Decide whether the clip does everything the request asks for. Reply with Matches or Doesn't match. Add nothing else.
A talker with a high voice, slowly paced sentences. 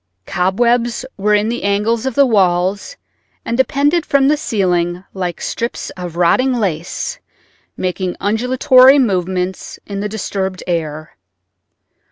Matches